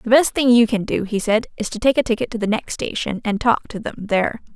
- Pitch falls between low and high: No, high, 225 Hz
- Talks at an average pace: No, fast, 290 wpm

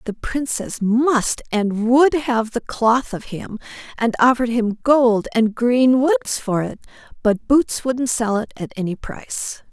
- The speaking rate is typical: Yes, average, 165 wpm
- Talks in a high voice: Yes, high, 240 Hz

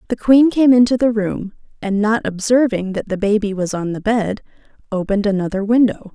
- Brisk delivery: No, average, 185 wpm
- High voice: Yes, high, 215 Hz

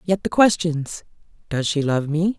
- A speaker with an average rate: Yes, average, 150 wpm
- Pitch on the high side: No, medium, 165 Hz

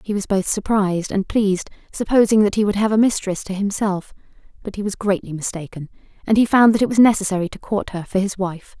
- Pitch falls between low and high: No, high, 200 Hz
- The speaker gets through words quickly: Yes, fast, 225 wpm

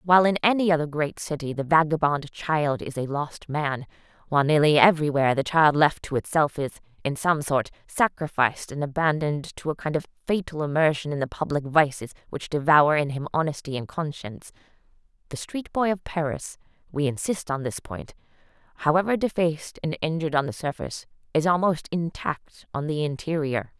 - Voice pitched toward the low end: No, medium, 150 Hz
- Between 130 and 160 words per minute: No, average, 170 wpm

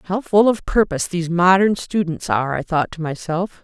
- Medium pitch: Yes, medium, 180 Hz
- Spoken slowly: No, average, 200 wpm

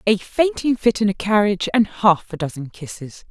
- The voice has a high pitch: Yes, high, 205 Hz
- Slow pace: No, average, 200 wpm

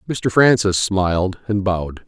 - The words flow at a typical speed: Yes, average, 145 wpm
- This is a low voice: Yes, low, 100 Hz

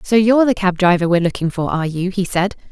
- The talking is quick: Yes, fast, 265 wpm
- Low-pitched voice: No, high, 190 Hz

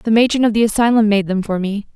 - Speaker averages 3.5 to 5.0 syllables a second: No, 6.5 syllables/s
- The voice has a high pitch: Yes, high, 215 Hz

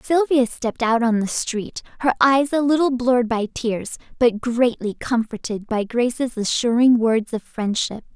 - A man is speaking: No, female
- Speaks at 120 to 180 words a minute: Yes, average, 160 wpm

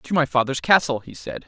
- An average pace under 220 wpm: No, fast, 245 wpm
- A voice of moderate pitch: Yes, medium, 145 Hz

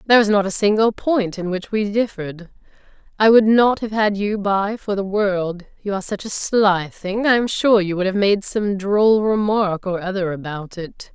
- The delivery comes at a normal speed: No, fast, 215 wpm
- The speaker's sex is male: No, female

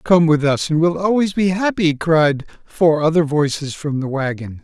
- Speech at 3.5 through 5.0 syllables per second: Yes, 4.6 syllables/s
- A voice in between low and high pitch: Yes, medium, 160 Hz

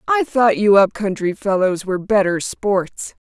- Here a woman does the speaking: Yes, female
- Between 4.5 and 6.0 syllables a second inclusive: No, 4.3 syllables/s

